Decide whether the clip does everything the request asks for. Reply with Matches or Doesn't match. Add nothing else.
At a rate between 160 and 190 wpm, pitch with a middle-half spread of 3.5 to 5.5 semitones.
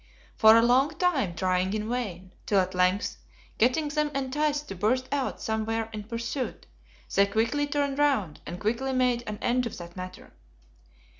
Matches